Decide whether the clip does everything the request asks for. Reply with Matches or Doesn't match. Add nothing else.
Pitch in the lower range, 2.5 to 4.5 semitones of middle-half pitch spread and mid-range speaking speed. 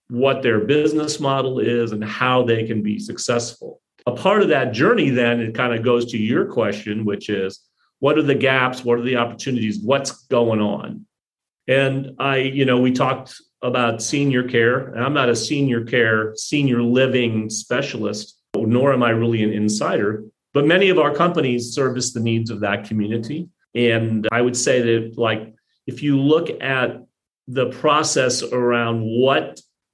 Matches